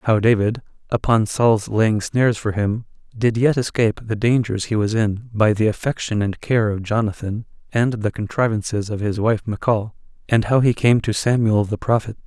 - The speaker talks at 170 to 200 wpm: Yes, average, 185 wpm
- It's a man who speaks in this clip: Yes, male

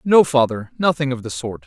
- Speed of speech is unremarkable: No, fast, 215 wpm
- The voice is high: No, medium, 140 Hz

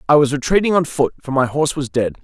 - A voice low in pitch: No, medium, 145 Hz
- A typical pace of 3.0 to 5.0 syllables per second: No, 6.6 syllables/s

